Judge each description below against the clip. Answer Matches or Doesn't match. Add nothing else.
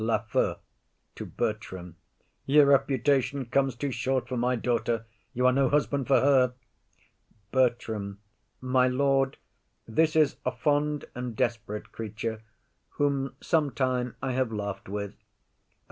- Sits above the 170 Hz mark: Doesn't match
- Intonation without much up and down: Doesn't match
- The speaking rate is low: Matches